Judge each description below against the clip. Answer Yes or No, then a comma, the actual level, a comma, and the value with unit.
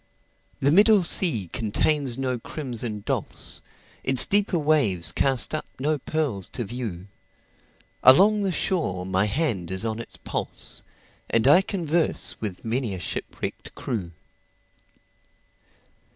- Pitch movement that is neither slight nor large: No, wide, 7.0 semitones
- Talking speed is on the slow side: Yes, slow, 110 wpm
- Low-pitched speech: Yes, low, 130 Hz